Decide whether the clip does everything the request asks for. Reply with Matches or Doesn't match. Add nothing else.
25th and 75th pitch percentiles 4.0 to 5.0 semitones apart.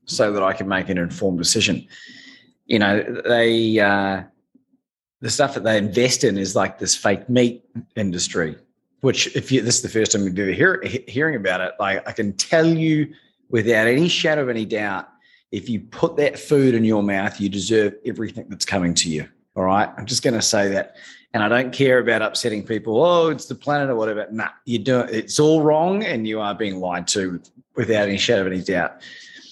Matches